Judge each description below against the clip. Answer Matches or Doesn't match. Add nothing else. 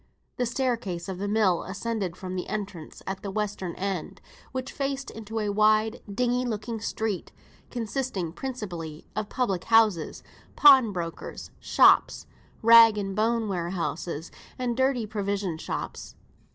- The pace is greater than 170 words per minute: Doesn't match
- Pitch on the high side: Matches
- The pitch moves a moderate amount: Matches